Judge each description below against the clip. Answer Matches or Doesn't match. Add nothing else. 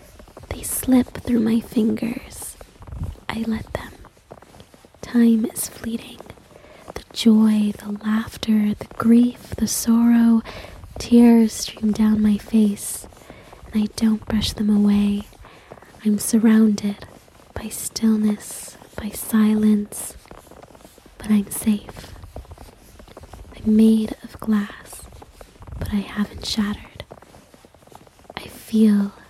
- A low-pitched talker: Doesn't match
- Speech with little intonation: Matches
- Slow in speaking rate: Matches